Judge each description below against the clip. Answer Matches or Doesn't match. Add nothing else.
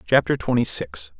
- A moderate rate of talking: Matches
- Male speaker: Matches